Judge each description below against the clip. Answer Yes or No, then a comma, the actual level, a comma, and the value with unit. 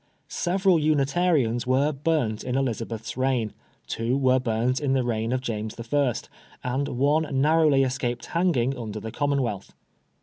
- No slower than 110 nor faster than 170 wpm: Yes, average, 140 wpm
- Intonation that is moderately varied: Yes, average, 3.5 semitones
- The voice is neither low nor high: No, low, 130 Hz